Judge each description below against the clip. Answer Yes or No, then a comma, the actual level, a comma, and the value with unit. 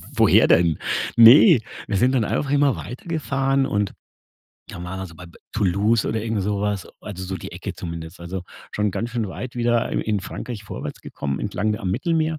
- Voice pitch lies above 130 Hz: No, low, 105 Hz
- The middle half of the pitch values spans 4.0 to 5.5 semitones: Yes, average, 4.9 semitones